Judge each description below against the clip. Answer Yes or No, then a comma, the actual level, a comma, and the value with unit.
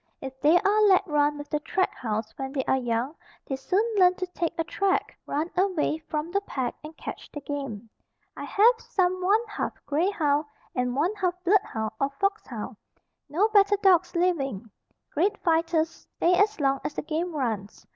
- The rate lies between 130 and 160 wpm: No, average, 185 wpm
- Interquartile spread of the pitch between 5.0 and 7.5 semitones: Yes, wide, 5.4 semitones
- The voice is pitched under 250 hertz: No, very high, 325 Hz